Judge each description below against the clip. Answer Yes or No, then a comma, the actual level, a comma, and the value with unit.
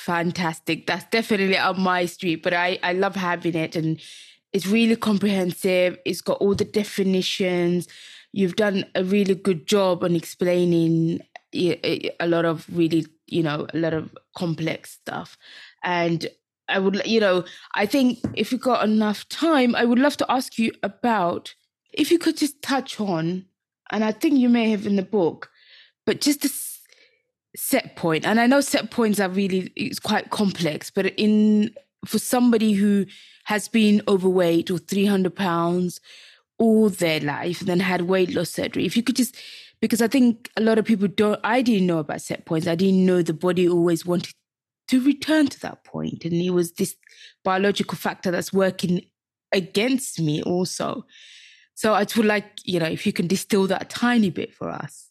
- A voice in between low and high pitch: No, high, 195 Hz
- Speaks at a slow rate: No, average, 180 wpm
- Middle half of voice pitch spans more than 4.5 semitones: No, average, 4.1 semitones